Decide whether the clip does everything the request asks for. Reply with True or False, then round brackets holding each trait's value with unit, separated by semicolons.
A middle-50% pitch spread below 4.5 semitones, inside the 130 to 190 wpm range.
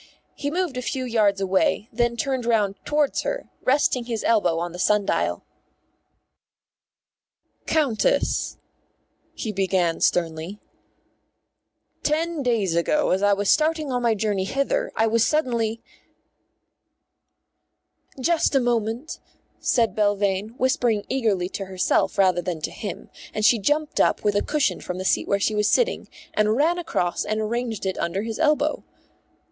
False (5.3 semitones; 150 wpm)